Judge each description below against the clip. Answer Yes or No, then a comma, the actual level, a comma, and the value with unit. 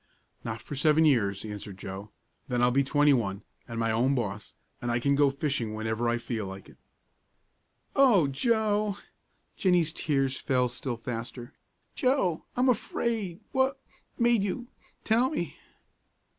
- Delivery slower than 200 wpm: Yes, average, 145 wpm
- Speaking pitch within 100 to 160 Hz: Yes, low, 135 Hz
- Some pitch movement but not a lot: No, wide, 9.0 semitones